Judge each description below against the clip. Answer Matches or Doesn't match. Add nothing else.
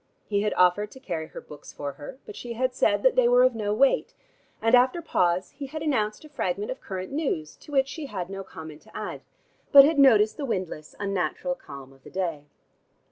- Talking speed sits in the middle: Doesn't match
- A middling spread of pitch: Doesn't match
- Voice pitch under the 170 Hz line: Doesn't match